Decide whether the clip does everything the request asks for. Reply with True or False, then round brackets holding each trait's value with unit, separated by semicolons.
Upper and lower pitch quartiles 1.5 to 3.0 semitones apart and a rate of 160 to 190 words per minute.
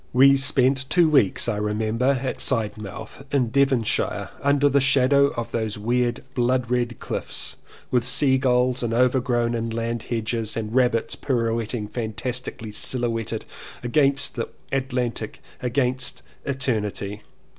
False (2.5 semitones; 135 wpm)